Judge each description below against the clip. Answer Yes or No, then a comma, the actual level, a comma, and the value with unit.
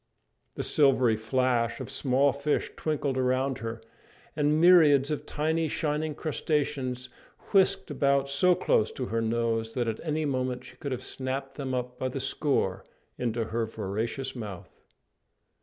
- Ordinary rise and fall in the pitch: Yes, average, 3.7 semitones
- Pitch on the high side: No, low, 130 Hz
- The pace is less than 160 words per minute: Yes, average, 150 wpm